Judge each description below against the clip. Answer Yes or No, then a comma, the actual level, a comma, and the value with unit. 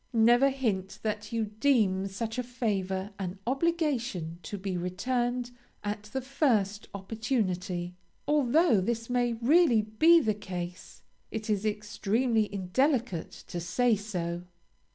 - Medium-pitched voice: No, high, 215 Hz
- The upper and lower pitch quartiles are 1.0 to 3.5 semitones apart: No, average, 4.4 semitones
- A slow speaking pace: Yes, slow, 125 wpm